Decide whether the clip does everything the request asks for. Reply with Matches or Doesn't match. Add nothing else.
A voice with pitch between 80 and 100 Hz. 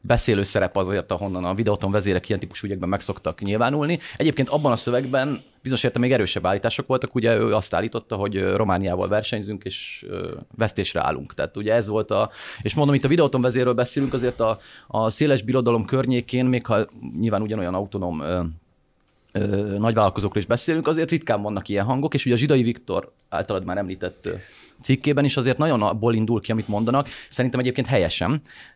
Doesn't match